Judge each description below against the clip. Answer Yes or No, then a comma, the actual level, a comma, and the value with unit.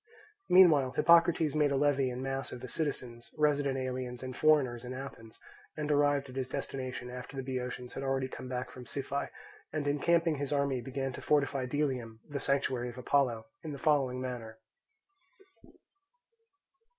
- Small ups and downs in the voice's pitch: Yes, narrow, 2.3 semitones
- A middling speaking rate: Yes, average, 160 wpm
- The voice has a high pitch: No, low, 135 Hz